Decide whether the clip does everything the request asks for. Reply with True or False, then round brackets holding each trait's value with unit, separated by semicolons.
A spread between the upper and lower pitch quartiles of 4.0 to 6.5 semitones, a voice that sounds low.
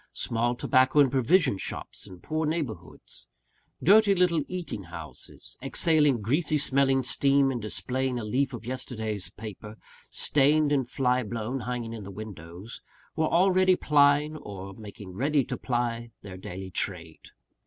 True (5.5 semitones; 125 Hz)